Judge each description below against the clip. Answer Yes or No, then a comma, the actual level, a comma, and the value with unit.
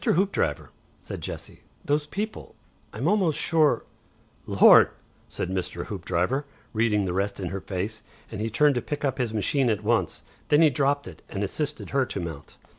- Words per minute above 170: Yes, average, 180 wpm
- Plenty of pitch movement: Yes, wide, 7.1 semitones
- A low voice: Yes, low, 115 Hz